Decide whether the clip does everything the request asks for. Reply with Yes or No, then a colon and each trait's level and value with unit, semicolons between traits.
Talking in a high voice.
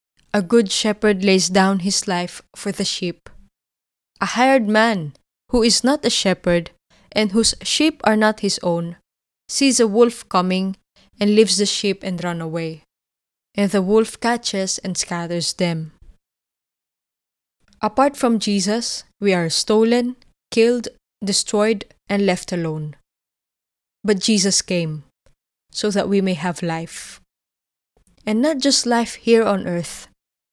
Yes: high, 200 Hz